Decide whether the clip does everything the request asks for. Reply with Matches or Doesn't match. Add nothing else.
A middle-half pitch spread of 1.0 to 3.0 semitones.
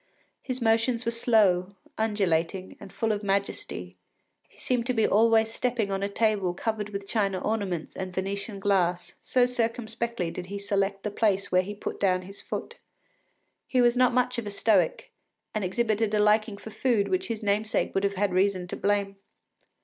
Matches